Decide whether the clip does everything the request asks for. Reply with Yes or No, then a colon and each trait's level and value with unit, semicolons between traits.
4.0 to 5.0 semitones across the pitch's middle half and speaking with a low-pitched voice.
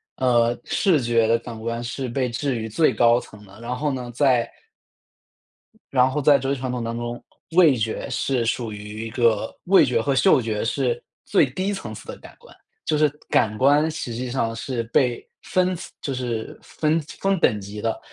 No: average, 3.3 semitones; low, 120 Hz